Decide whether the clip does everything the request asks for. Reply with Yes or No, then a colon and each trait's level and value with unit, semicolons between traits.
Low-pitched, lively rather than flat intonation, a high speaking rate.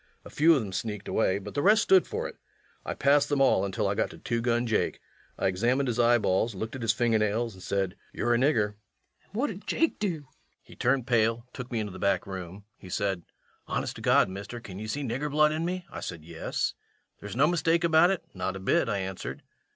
Yes: low, 115 Hz; wide, 6.7 semitones; fast, 240 wpm